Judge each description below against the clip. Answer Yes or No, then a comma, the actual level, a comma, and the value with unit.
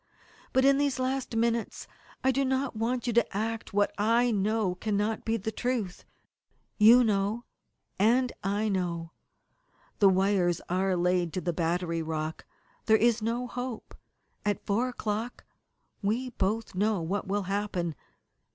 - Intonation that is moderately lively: Yes, average, 3.9 semitones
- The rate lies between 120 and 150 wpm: Yes, average, 145 wpm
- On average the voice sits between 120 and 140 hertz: No, high, 215 Hz